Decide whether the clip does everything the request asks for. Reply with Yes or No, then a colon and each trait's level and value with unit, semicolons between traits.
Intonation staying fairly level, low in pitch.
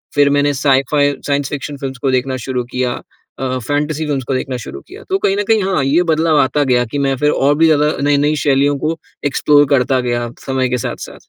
No: narrow, 2.1 semitones; medium, 145 Hz